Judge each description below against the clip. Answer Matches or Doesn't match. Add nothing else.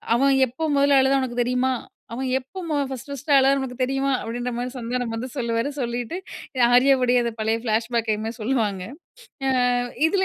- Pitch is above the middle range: Matches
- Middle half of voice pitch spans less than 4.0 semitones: Matches